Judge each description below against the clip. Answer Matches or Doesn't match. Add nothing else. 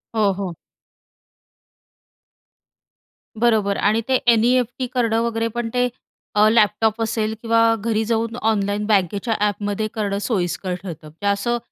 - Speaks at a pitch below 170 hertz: Doesn't match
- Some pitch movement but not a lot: Doesn't match